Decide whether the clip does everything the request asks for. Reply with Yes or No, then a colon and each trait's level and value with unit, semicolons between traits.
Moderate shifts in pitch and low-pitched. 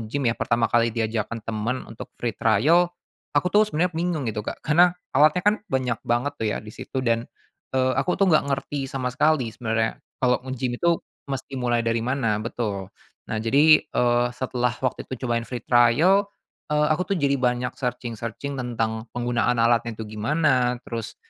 Yes: average, 3.6 semitones; low, 125 Hz